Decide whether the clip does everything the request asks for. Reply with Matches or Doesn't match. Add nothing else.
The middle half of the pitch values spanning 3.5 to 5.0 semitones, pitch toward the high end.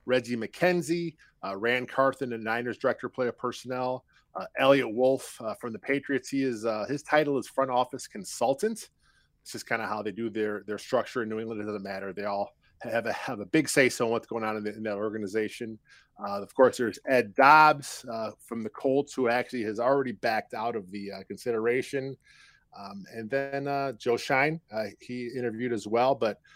Doesn't match